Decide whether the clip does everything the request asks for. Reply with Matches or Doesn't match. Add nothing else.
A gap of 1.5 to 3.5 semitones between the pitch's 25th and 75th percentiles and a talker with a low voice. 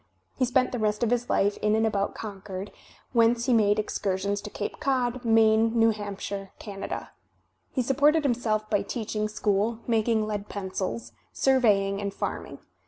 Doesn't match